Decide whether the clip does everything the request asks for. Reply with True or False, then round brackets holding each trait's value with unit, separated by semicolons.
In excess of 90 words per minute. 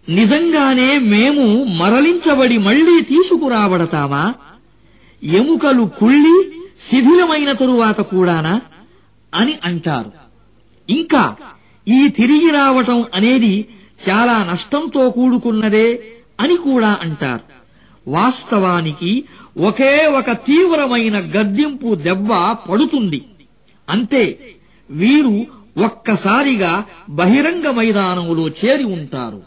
False (75 wpm)